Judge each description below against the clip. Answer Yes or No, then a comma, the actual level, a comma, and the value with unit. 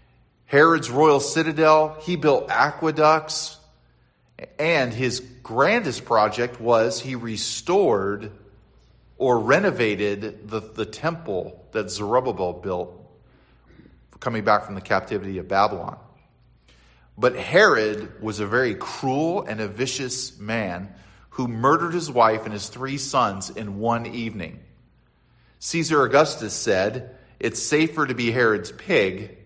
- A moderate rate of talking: No, slow, 120 wpm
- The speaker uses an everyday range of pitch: Yes, average, 5.0 semitones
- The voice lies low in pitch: Yes, low, 115 Hz